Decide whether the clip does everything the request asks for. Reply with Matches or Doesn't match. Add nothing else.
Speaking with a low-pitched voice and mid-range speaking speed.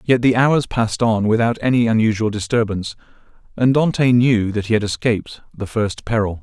Matches